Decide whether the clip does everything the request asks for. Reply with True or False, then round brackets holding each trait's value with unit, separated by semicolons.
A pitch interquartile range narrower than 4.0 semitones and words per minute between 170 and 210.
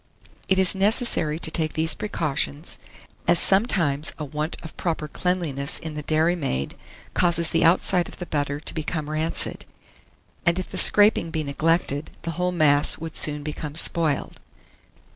False (2.6 semitones; 155 wpm)